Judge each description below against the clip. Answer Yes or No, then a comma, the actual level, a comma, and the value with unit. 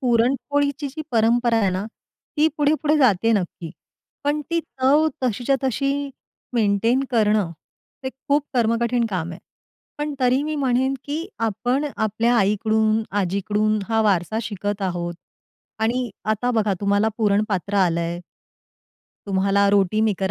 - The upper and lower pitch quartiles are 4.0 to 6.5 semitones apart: Yes, average, 4.6 semitones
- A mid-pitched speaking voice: No, high, 225 Hz